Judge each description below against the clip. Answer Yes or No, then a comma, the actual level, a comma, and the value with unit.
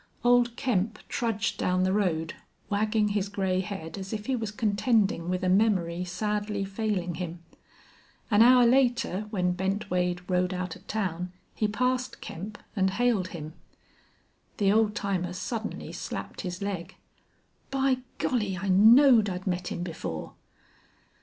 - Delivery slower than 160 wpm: Yes, average, 145 wpm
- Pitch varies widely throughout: No, average, 3.3 semitones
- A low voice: No, high, 200 Hz